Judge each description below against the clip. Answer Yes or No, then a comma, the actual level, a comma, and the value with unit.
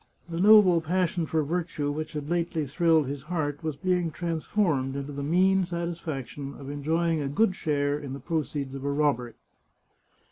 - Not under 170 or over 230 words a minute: Yes, average, 175 wpm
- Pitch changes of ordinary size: Yes, average, 3.3 semitones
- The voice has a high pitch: No, medium, 155 Hz